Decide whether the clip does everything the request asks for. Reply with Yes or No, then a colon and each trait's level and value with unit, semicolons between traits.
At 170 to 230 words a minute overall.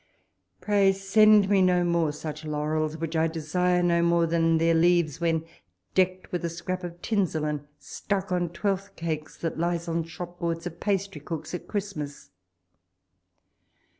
No: average, 155 wpm